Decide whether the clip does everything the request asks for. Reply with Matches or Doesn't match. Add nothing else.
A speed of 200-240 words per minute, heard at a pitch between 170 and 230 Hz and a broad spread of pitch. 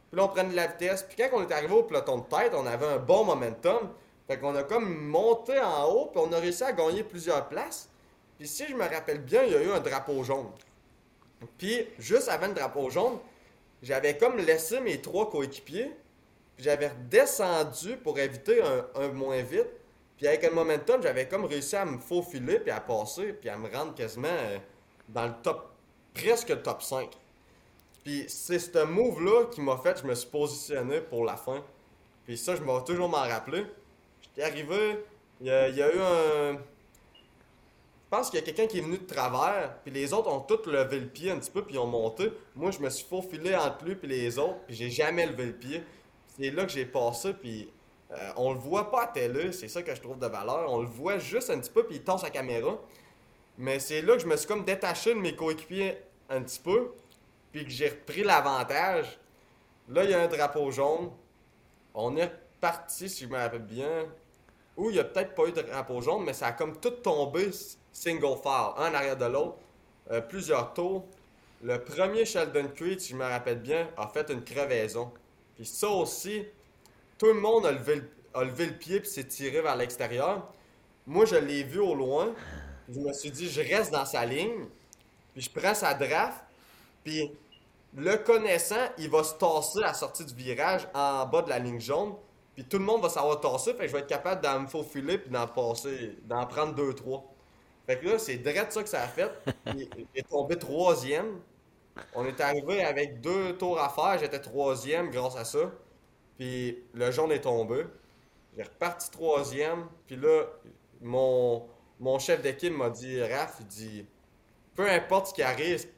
Doesn't match